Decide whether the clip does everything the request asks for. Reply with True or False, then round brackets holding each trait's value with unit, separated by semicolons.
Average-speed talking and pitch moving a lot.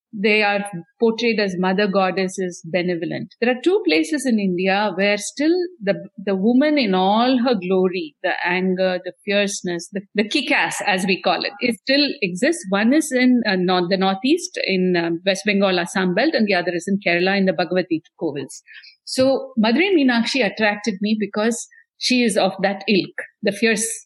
False (180 wpm; 4.6 semitones)